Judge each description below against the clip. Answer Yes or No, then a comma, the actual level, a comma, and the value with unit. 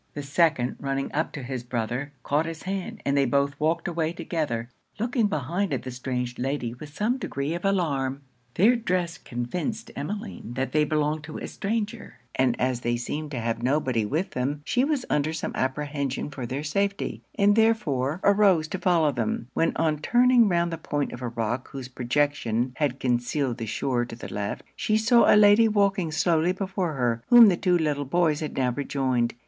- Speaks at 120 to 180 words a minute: No, average, 190 wpm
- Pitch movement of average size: No, wide, 6.1 semitones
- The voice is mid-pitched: Yes, medium, 150 Hz